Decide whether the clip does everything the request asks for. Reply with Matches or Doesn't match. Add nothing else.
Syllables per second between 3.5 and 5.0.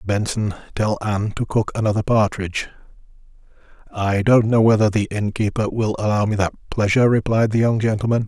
Doesn't match